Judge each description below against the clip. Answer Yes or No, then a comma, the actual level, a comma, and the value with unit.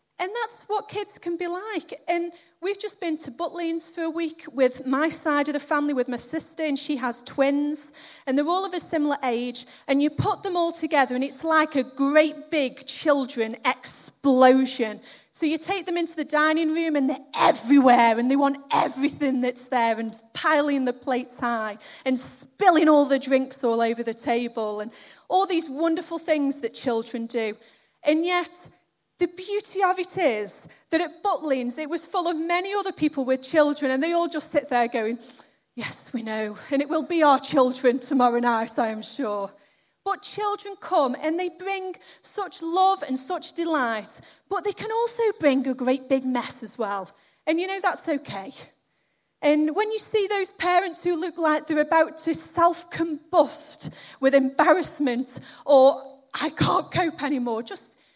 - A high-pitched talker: Yes, very high, 300 Hz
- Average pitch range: Yes, average, 4.7 semitones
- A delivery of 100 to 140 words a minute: No, average, 185 wpm